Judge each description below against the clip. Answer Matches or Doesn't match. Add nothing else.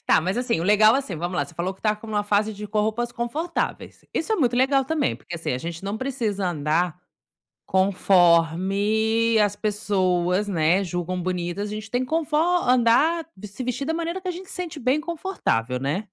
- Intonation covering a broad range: Matches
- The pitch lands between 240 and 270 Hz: Doesn't match